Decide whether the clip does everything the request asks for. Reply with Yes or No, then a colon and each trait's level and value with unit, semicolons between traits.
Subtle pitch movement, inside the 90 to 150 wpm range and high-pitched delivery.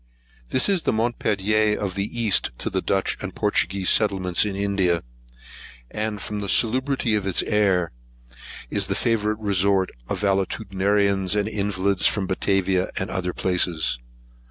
No: narrow, 2.0 semitones; average, 145 wpm; low, 100 Hz